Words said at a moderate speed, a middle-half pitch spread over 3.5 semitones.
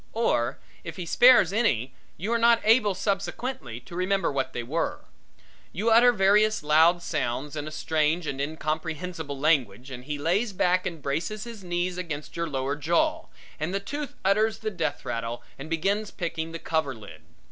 Yes: average, 175 wpm; wide, 5.6 semitones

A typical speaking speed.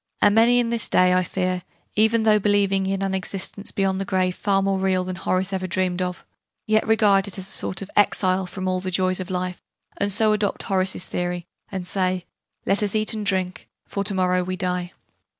No: fast, 215 wpm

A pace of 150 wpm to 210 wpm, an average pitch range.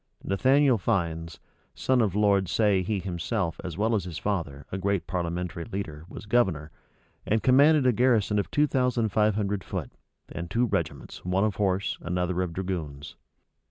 Yes: average, 165 wpm; average, 4.1 semitones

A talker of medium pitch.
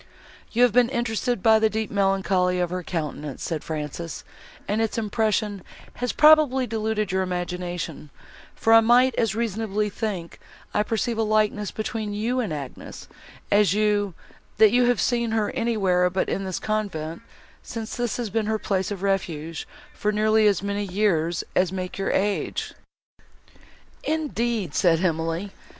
No: high, 210 Hz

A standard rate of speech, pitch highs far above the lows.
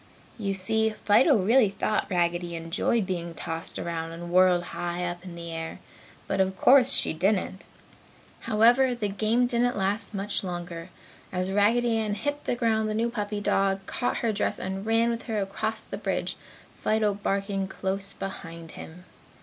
No: average, 165 wpm; average, 3.7 semitones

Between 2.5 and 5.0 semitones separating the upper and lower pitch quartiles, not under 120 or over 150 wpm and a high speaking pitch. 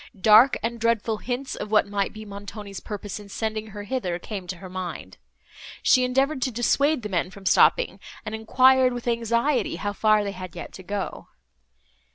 No: average, 3.4 semitones; average, 185 wpm; high, 215 Hz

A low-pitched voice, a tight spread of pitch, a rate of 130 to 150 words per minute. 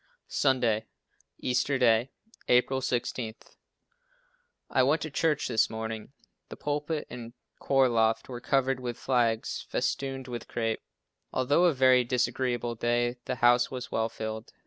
Yes: low, 125 Hz; narrow, 2.3 semitones; slow, 135 wpm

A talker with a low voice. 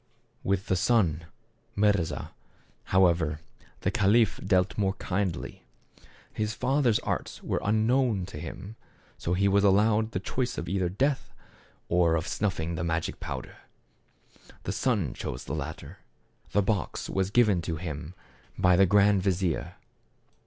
Yes: very low, 95 Hz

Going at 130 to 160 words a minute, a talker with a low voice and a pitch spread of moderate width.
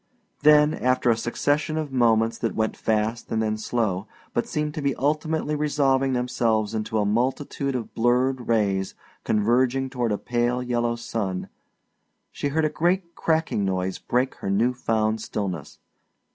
Yes: average, 155 wpm; low, 120 Hz; average, 4.0 semitones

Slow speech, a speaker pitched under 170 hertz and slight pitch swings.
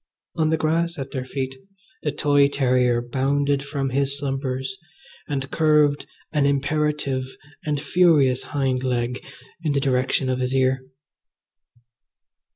Yes: slow, 130 wpm; medium, 140 Hz; narrow, 2.2 semitones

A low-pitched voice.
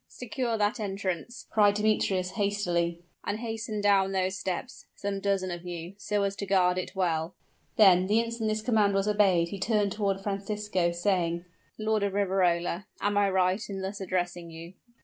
No: high, 195 Hz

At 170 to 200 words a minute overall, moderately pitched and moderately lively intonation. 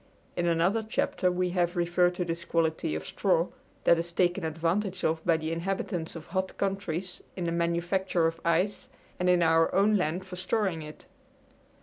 No: average, 180 wpm; medium, 175 Hz; narrow, 2.0 semitones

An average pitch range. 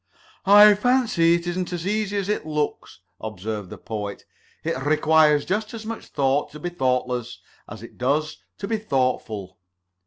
No: wide, 8.0 semitones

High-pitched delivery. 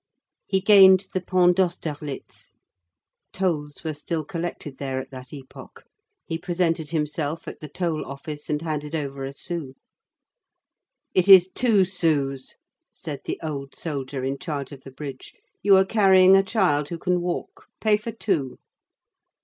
No: medium, 160 Hz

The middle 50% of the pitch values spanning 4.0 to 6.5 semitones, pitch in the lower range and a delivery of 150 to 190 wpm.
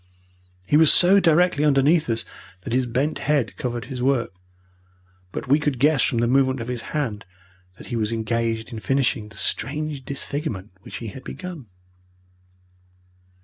Yes: average, 4.3 semitones; low, 130 Hz; average, 160 wpm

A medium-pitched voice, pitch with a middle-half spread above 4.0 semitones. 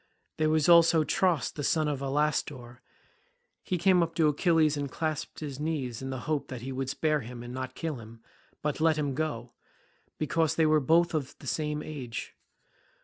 No: medium, 150 Hz; average, 3.3 semitones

